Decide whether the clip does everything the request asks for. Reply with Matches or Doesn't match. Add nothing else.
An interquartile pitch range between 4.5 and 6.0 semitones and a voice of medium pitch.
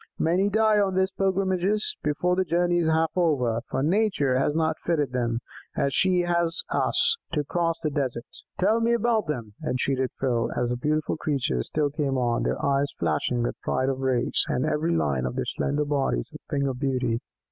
Matches